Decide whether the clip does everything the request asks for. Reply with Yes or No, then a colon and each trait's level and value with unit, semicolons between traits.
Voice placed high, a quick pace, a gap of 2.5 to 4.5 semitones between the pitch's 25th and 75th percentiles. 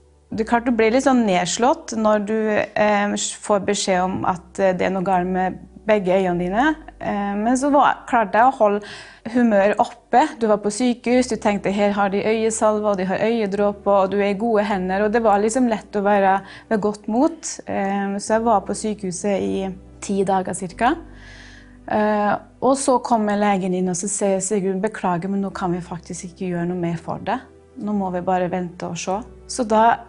Yes: high, 205 Hz; fast, 210 wpm; average, 2.9 semitones